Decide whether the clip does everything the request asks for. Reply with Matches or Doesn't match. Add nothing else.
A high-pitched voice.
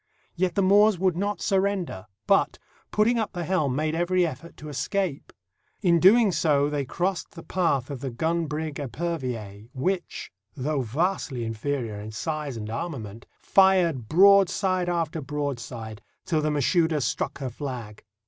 Doesn't match